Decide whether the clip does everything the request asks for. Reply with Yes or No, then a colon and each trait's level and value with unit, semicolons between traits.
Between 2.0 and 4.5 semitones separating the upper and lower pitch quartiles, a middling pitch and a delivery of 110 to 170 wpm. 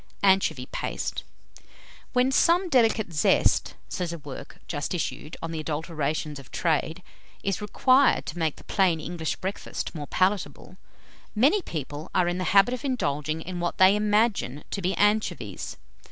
No: average, 5.1 semitones; medium, 180 Hz; average, 155 wpm